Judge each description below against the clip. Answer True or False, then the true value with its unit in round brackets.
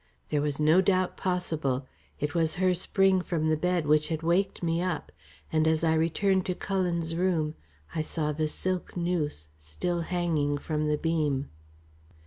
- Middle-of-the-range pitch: True (165 Hz)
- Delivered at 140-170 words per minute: True (165 wpm)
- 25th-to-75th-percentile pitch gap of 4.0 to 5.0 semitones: False (2.9 semitones)